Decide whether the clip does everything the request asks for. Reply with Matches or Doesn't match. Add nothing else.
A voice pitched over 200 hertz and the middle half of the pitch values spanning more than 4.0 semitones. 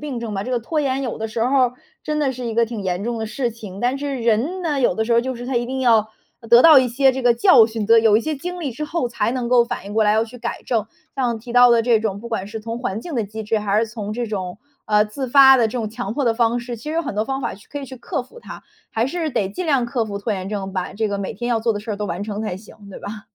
Doesn't match